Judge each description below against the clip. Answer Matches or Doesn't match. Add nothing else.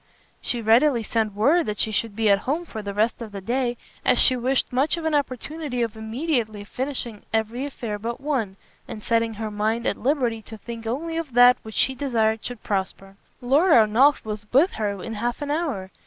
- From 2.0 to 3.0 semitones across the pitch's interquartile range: Doesn't match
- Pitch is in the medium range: Doesn't match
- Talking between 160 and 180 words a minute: Doesn't match